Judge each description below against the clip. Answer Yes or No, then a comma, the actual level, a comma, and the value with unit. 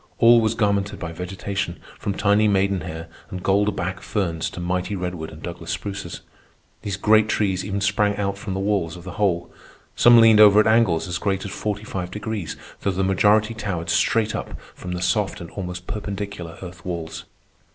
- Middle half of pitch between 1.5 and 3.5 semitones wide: Yes, average, 2.7 semitones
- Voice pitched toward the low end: Yes, low, 100 Hz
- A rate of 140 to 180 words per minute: No, average, 190 wpm